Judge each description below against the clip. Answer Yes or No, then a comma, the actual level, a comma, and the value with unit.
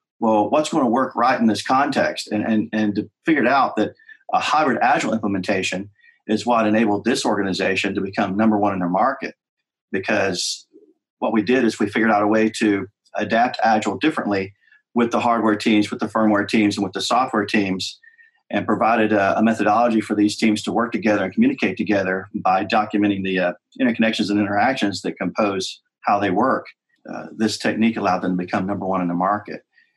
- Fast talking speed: No, average, 195 wpm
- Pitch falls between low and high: No, low, 105 Hz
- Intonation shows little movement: Yes, narrow, 1.9 semitones